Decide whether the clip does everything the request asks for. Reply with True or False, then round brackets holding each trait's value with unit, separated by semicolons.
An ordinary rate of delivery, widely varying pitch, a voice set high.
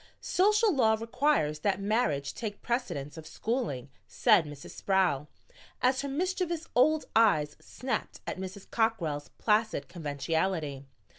False (125 wpm; 8.9 semitones; 205 Hz)